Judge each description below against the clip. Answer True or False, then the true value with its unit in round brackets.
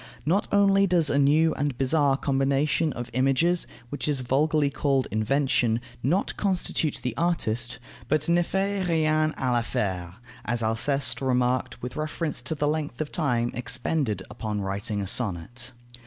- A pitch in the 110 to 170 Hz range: True (135 Hz)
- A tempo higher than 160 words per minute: False (150 wpm)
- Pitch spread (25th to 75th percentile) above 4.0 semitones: True (4.5 semitones)